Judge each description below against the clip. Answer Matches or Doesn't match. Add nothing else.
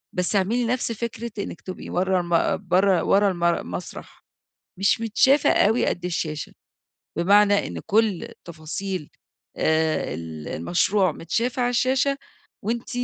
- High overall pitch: Matches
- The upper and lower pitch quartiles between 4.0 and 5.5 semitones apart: Matches